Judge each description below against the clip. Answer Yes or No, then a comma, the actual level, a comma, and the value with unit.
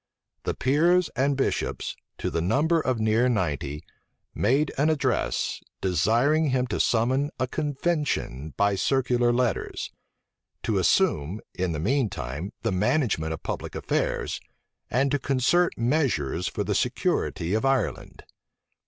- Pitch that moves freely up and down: Yes, wide, 7.2 semitones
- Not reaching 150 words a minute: Yes, slow, 135 wpm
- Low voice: Yes, low, 125 Hz